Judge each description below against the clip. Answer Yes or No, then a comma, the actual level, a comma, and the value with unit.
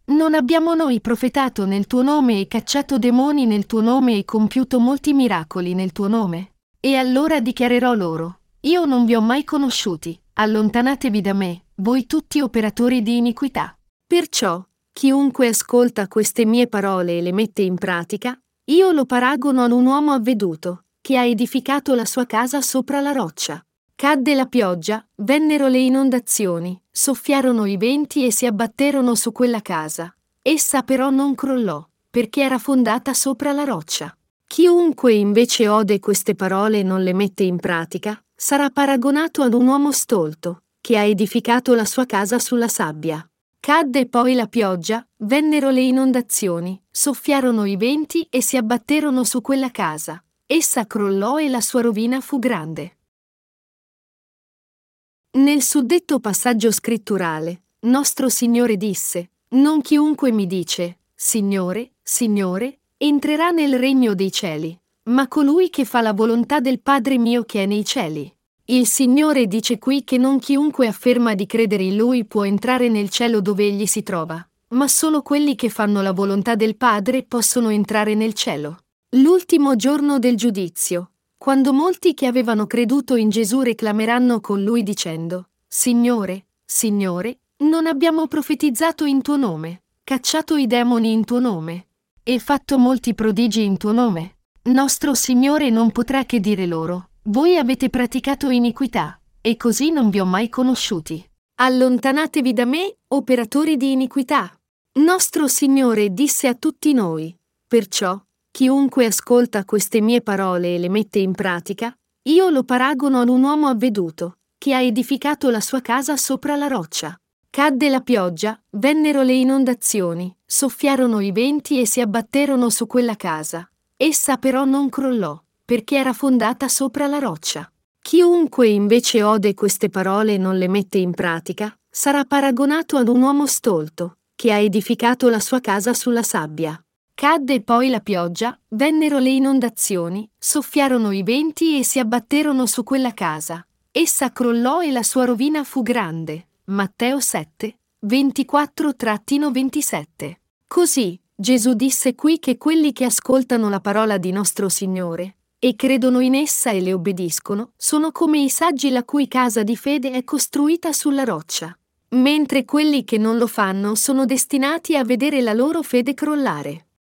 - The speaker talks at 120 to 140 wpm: No, average, 150 wpm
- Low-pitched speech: No, high, 245 Hz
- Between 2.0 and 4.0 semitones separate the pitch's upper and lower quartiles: No, average, 4.7 semitones